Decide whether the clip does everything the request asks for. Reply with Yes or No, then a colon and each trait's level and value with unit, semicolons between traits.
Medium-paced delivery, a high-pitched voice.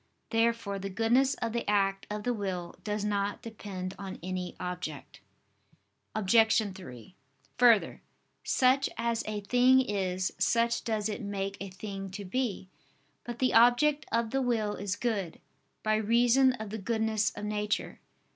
Yes: average, 150 wpm; high, 210 Hz